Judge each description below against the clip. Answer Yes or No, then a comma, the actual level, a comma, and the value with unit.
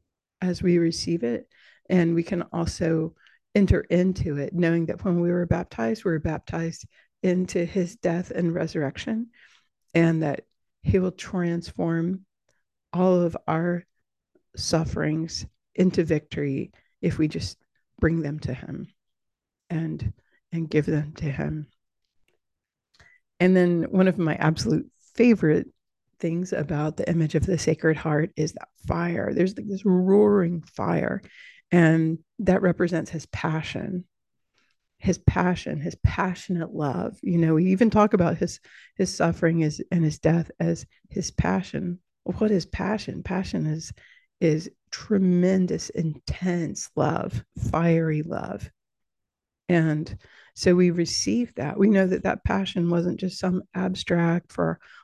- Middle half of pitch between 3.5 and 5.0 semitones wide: No, narrow, 2.5 semitones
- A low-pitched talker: No, medium, 170 Hz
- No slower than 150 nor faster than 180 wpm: No, slow, 135 wpm